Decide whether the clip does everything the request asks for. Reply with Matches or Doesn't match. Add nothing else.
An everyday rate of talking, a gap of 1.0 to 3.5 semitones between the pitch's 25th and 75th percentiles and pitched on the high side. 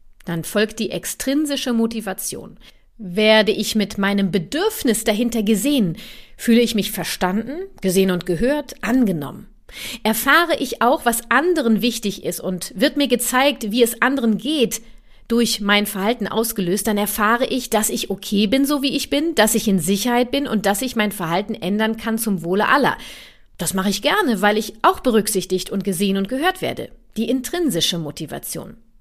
Doesn't match